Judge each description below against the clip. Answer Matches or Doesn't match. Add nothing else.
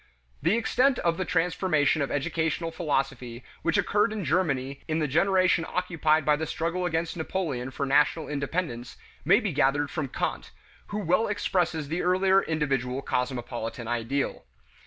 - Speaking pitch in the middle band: Matches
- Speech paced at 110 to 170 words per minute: Matches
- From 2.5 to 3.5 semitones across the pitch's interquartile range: Doesn't match